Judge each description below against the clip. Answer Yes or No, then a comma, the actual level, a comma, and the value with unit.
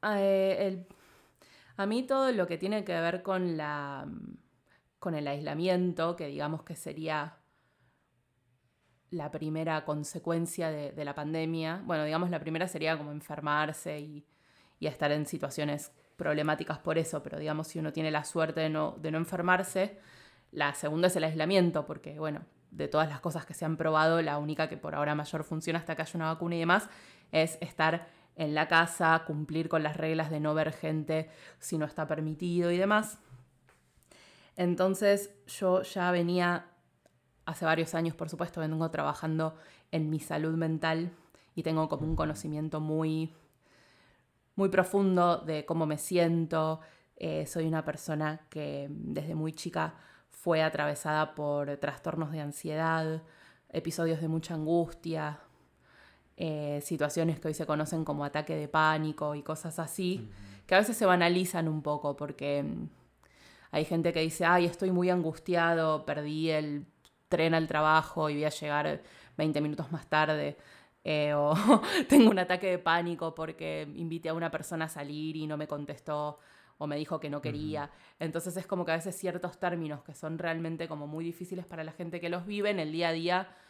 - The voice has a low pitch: No, medium, 160 Hz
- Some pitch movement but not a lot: No, narrow, 2.1 semitones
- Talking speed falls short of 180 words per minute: Yes, average, 170 wpm